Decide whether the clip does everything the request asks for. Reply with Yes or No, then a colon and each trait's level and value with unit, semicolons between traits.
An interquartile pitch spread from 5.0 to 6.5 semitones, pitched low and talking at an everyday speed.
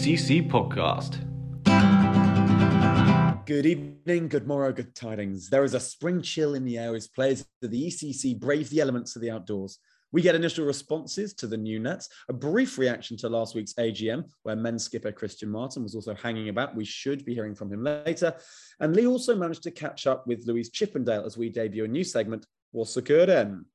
Yes: average, 5.3 semitones; low, 130 Hz; average, 190 wpm